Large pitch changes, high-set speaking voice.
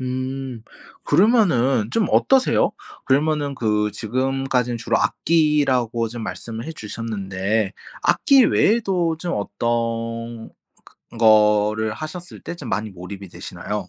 No: wide, 5.7 semitones; low, 120 Hz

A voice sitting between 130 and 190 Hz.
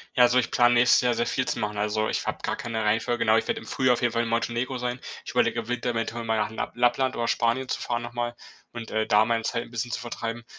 No: low, 120 Hz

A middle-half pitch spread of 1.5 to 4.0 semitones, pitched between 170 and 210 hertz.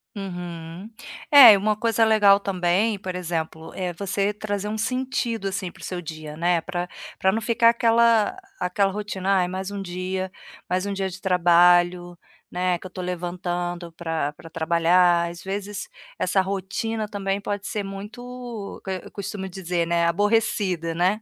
Yes: average, 2.7 semitones; high, 190 Hz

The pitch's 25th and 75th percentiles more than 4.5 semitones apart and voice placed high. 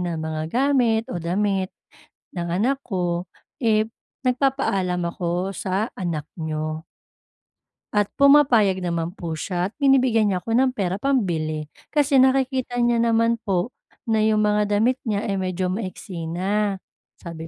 Yes: average, 5.0 semitones; high, 200 Hz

